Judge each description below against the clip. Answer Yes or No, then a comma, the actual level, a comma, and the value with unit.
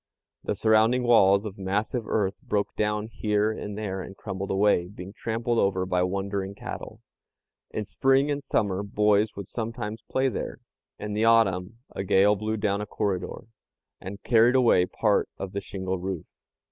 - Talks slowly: No, average, 165 wpm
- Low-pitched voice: Yes, low, 105 Hz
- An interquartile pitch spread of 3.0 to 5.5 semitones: No, narrow, 2.4 semitones